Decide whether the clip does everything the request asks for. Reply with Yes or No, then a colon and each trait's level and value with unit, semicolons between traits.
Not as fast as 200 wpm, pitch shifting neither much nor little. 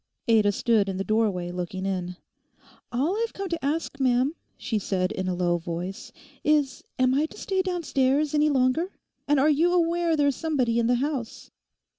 No: average, 180 wpm; wide, 7.5 semitones